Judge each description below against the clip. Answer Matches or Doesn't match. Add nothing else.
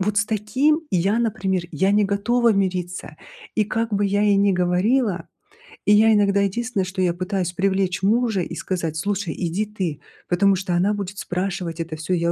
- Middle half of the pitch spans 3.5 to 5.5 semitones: Doesn't match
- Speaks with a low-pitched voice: Doesn't match